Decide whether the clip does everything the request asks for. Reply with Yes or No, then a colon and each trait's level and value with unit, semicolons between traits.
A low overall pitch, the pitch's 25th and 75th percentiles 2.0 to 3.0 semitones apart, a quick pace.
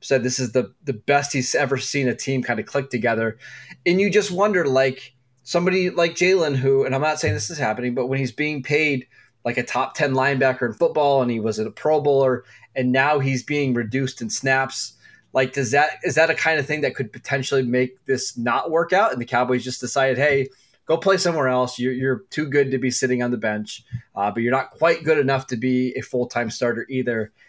Yes: low, 130 Hz; narrow, 2.6 semitones; fast, 235 wpm